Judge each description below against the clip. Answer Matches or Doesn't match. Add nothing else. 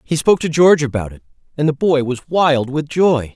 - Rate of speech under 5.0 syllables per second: Doesn't match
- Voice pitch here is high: Doesn't match